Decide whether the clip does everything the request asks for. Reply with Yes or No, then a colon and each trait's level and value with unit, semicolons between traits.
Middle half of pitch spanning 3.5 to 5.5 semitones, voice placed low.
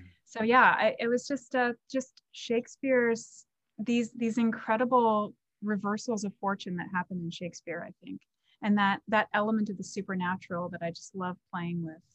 No: average, 4.5 semitones; high, 210 Hz